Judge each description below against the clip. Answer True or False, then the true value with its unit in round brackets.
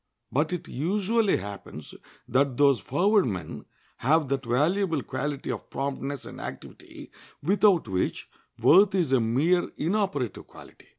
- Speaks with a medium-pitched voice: True (145 Hz)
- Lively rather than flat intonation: True (6.2 semitones)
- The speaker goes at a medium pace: False (130 wpm)